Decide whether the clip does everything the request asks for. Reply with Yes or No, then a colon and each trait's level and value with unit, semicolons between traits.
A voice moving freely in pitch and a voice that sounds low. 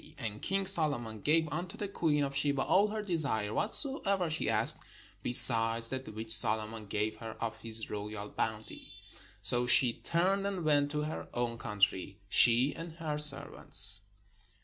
Yes: wide, 6.7 semitones; low, 130 Hz